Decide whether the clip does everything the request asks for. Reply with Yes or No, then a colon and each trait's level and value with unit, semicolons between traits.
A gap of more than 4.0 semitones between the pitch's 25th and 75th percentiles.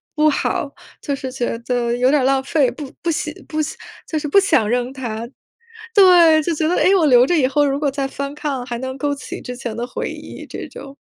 No: average, 3.4 semitones